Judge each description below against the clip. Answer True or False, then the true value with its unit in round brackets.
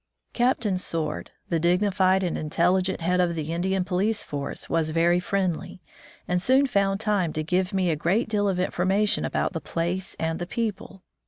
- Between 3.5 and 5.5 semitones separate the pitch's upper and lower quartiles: False (2.6 semitones)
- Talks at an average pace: True (180 wpm)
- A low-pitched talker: False (185 Hz)